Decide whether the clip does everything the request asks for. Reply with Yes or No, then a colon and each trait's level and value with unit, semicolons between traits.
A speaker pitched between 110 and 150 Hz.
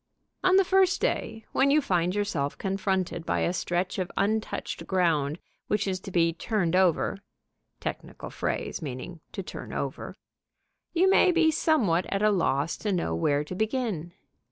No: high, 190 Hz